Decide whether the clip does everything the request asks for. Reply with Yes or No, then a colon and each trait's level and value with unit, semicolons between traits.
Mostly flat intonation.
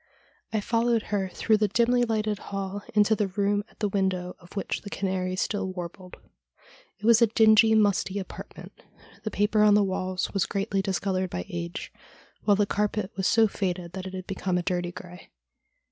Yes: narrow, 2.3 semitones